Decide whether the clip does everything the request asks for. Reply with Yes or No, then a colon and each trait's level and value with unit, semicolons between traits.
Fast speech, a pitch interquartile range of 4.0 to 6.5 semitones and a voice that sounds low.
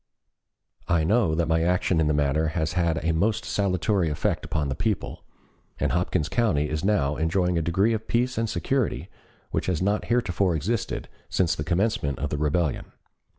No: average, 180 wpm; average, 4.5 semitones; very low, 85 Hz